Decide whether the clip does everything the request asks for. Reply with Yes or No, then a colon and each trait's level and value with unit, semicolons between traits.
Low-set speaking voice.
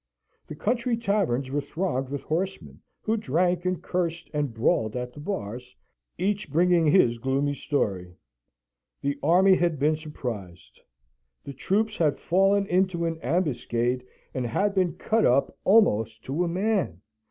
No: medium, 155 Hz